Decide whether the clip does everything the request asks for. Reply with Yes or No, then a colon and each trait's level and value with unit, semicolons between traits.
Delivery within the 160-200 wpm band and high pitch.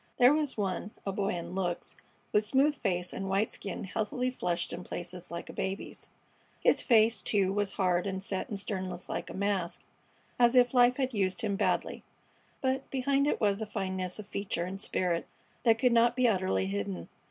Yes: average, 190 wpm; high, 200 Hz